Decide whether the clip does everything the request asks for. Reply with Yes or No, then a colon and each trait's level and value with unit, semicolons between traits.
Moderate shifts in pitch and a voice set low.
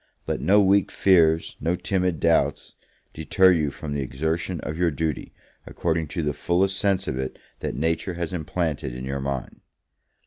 Yes: average, 3.5 semitones; very low, 80 Hz